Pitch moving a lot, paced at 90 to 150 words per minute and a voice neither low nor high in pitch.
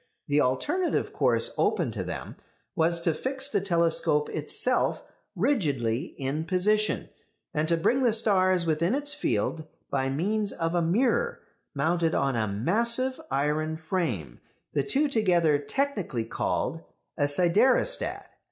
Yes: wide, 7.0 semitones; slow, 135 wpm; medium, 170 Hz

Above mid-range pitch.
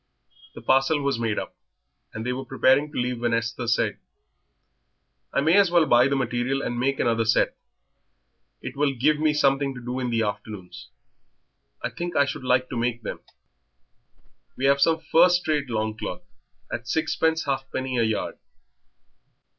No: low, 130 Hz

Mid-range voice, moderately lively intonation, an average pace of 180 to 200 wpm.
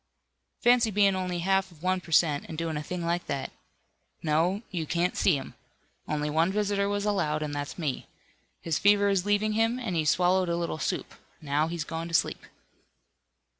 Yes: medium, 175 Hz; average, 4.1 semitones; average, 190 wpm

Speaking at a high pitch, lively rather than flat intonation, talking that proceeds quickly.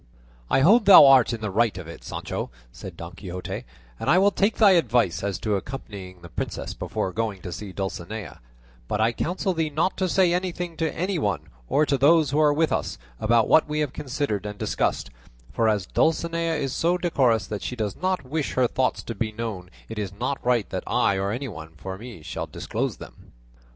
No: low, 120 Hz; wide, 8.1 semitones; fast, 210 wpm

